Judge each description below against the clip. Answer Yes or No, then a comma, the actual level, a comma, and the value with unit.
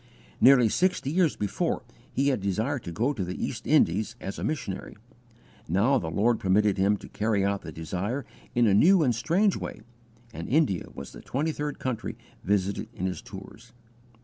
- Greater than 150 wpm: Yes, average, 180 wpm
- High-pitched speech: No, low, 110 Hz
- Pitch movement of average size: No, wide, 6.2 semitones